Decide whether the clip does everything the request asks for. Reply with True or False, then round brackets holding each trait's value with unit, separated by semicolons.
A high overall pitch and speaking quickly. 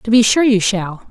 True (215 Hz; 270 wpm)